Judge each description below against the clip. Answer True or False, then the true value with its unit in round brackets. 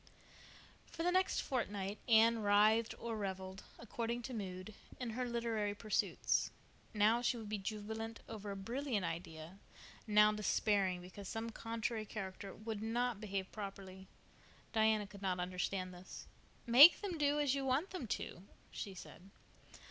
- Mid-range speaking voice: False (215 Hz)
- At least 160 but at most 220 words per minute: False (150 wpm)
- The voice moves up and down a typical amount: True (3.1 semitones)